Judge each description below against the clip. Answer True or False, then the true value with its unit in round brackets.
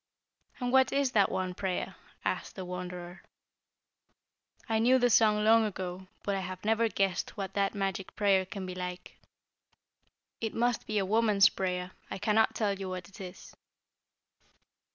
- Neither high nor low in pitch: False (195 Hz)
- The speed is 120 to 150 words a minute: False (160 wpm)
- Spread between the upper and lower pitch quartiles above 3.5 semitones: False (3.0 semitones)